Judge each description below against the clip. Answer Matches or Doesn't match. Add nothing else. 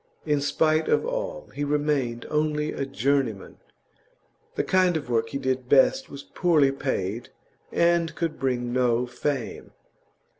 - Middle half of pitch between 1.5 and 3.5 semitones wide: Doesn't match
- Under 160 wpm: Matches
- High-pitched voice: Doesn't match